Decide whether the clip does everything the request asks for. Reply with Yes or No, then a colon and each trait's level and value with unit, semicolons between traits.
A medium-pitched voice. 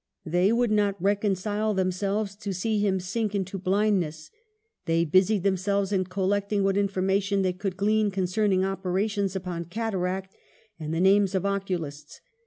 No: high, 195 Hz